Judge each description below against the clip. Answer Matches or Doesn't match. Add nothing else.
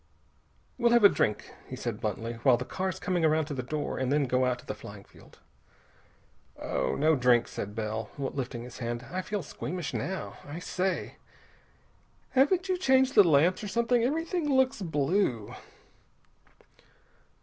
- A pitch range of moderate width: Doesn't match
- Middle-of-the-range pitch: Matches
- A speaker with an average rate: Matches